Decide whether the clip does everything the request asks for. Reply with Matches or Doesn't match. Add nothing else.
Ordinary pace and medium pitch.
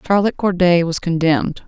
Matches